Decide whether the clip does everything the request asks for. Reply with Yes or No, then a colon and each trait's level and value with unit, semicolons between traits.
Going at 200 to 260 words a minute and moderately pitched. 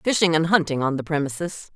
Yes: fast, 205 wpm; medium, 160 Hz